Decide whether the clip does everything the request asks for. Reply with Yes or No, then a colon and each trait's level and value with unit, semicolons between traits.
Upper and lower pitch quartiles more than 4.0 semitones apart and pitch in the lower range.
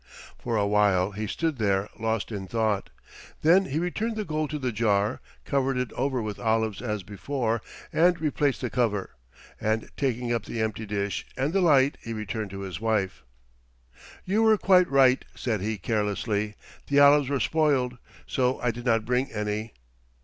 Yes: average, 4.9 semitones; low, 115 Hz